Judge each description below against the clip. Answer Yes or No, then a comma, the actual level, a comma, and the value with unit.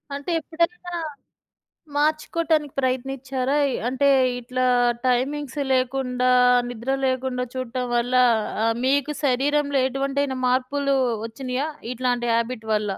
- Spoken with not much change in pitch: Yes, narrow, 2.1 semitones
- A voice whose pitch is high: Yes, very high, 260 Hz